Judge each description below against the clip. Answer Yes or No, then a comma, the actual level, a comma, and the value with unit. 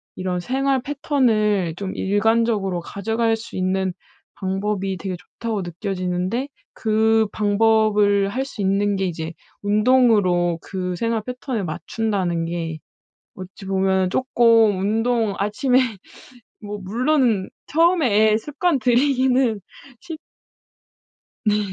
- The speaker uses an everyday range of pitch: Yes, average, 3.8 semitones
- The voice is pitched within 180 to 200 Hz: No, high, 210 Hz